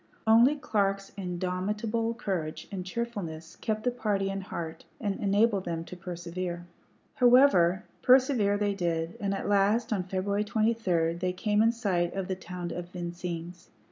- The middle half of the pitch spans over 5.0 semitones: No, average, 3.5 semitones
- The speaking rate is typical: Yes, average, 150 wpm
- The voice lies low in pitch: No, high, 195 Hz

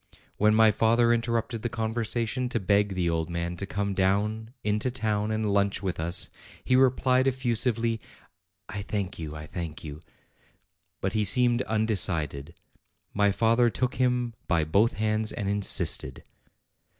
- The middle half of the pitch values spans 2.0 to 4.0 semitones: Yes, average, 3.4 semitones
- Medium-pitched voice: No, low, 105 Hz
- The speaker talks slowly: No, average, 150 wpm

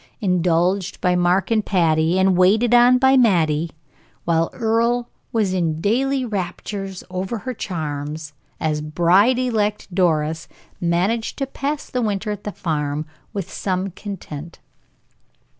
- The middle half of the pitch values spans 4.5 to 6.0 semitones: Yes, average, 5.0 semitones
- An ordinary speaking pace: No, slow, 130 wpm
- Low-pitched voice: No, high, 190 Hz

